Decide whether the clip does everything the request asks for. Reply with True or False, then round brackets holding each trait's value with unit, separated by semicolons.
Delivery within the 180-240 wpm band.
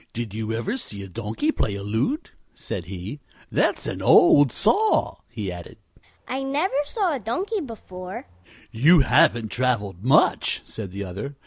False (165 wpm)